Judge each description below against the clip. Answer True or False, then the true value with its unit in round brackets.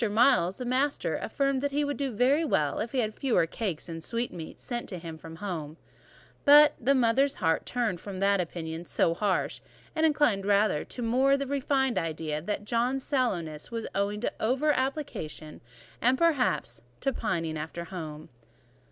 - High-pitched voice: True (220 Hz)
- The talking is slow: False (170 wpm)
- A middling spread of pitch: False (8.1 semitones)